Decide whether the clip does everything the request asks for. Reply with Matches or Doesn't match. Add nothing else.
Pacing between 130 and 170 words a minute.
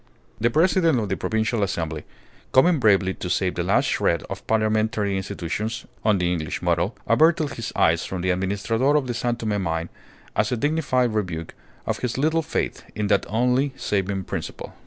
Doesn't match